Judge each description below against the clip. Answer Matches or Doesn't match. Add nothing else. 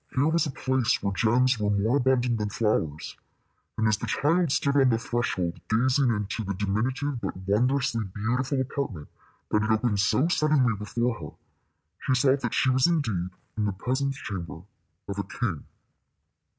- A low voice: Matches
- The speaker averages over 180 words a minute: Doesn't match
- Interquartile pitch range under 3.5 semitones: Doesn't match